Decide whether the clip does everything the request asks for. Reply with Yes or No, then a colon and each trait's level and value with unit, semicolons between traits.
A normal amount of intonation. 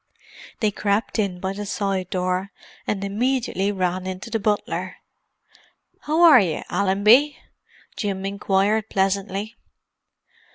No: narrow, 2.2 semitones